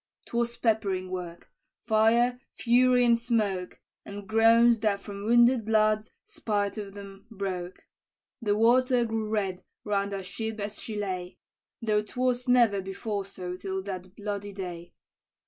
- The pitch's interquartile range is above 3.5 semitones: No, average, 2.9 semitones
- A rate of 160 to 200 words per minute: No, average, 140 wpm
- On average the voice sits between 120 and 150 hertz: No, high, 210 Hz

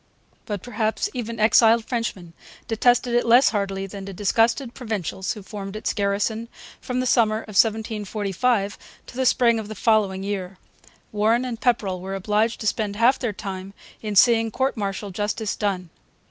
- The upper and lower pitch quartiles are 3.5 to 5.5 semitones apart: No, average, 2.8 semitones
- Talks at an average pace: Yes, average, 165 wpm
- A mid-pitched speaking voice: No, high, 215 Hz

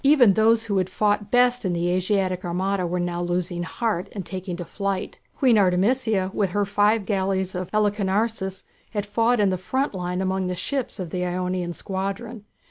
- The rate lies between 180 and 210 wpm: Yes, average, 185 wpm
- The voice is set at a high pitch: Yes, high, 195 Hz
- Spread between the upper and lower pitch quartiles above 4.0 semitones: No, average, 2.7 semitones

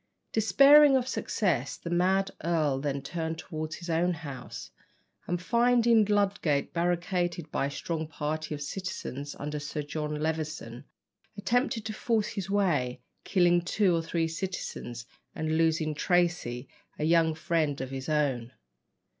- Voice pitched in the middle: Yes, medium, 165 Hz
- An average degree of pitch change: Yes, average, 4.1 semitones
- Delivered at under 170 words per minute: Yes, average, 140 wpm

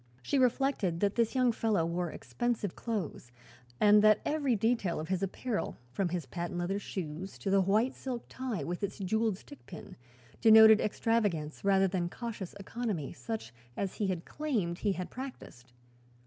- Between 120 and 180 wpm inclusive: Yes, average, 165 wpm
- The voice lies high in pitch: Yes, high, 200 Hz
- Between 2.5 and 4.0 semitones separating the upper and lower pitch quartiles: No, average, 4.7 semitones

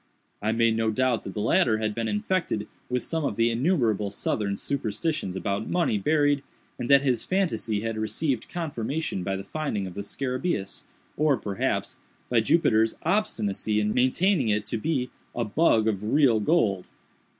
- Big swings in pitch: Yes, wide, 5.8 semitones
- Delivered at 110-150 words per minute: No, average, 165 wpm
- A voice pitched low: Yes, low, 115 Hz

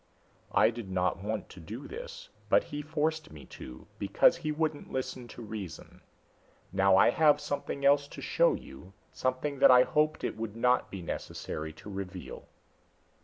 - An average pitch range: No, wide, 7.2 semitones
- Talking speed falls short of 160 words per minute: No, average, 170 wpm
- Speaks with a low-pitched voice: Yes, low, 125 Hz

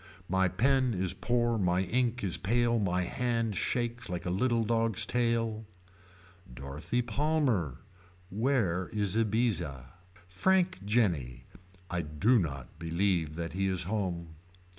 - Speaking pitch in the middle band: No, low, 100 Hz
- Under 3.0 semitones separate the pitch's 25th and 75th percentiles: No, average, 5.3 semitones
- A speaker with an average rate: No, slow, 125 wpm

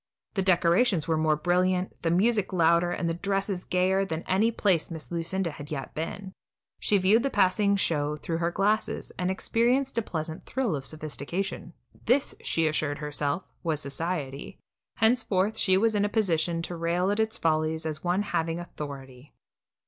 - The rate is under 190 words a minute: Yes, average, 170 wpm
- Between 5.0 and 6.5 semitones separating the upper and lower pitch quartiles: No, average, 3.9 semitones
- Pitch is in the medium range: Yes, medium, 175 Hz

